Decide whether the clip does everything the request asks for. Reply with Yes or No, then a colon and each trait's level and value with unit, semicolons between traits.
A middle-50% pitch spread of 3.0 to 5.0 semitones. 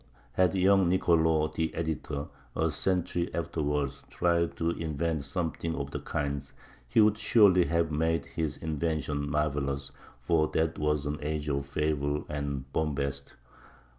No: narrow, 2.5 semitones